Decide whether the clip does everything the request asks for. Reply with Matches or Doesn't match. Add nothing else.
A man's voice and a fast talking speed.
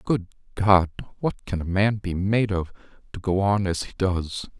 Doesn't match